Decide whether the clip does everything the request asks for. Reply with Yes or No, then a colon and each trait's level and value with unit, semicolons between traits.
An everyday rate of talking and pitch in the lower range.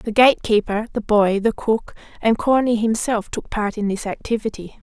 No: average, 185 wpm; high, 220 Hz